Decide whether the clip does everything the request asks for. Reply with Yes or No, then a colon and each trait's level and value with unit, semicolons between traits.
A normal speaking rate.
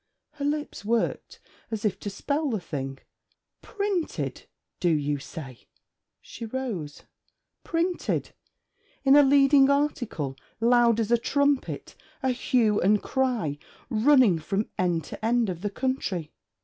No: slow, 130 wpm